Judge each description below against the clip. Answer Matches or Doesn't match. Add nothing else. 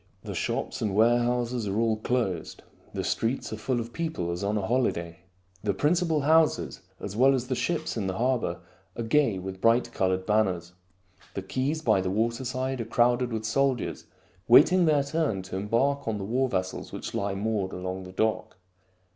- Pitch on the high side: Doesn't match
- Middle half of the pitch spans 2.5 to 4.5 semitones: Doesn't match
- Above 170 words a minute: Matches